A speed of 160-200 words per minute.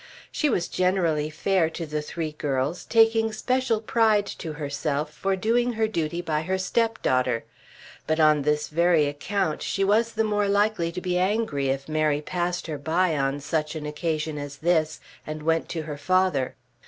Yes: average, 175 wpm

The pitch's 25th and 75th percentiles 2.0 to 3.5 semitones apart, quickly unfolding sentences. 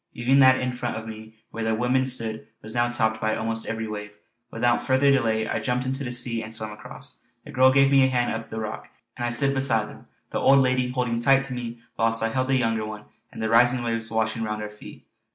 Yes: narrow, 2.6 semitones; fast, 245 wpm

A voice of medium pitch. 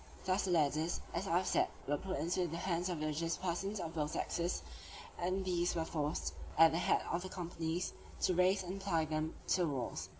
Yes: medium, 170 Hz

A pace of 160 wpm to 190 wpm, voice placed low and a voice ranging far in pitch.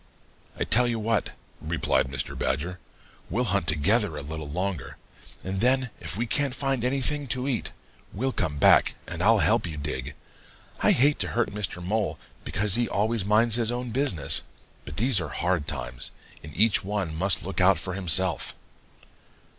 Yes: average, 170 wpm; low, 100 Hz; wide, 6.3 semitones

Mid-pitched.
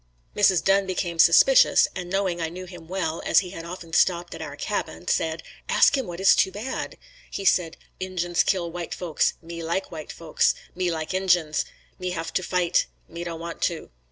Yes: medium, 175 Hz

